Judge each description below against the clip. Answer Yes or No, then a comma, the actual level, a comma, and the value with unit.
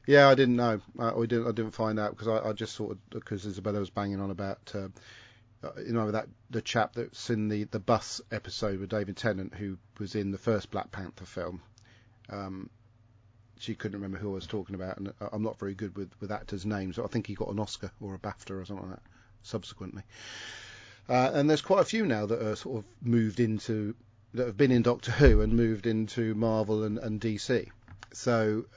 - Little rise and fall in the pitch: Yes, narrow, 2.1 semitones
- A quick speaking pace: Yes, fast, 215 wpm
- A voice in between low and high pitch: No, low, 110 Hz